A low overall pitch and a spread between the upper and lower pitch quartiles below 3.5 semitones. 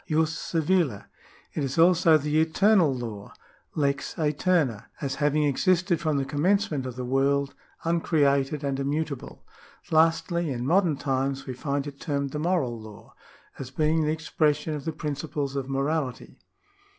No: medium, 150 Hz; average, 2.9 semitones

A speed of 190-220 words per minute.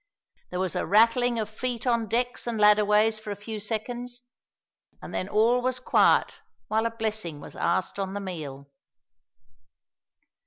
No: average, 155 wpm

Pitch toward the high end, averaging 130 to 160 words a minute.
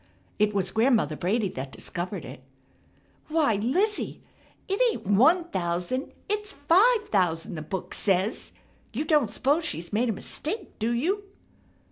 Yes: high, 230 Hz; average, 140 wpm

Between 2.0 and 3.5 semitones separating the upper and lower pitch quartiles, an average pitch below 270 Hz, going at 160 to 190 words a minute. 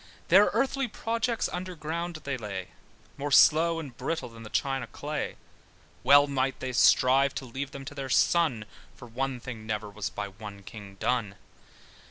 No: wide, 5.4 semitones; low, 135 Hz; average, 170 wpm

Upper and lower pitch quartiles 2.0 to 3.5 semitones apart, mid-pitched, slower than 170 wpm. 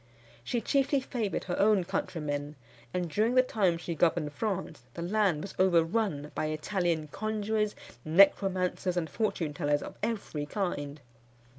No: wide, 5.4 semitones; medium, 180 Hz; average, 140 wpm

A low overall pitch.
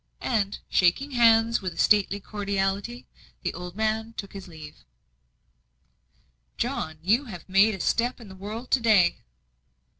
No: high, 205 Hz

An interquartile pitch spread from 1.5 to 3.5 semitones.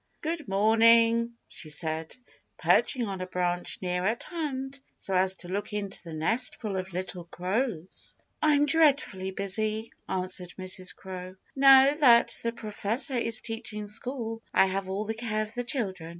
No: average, 4.2 semitones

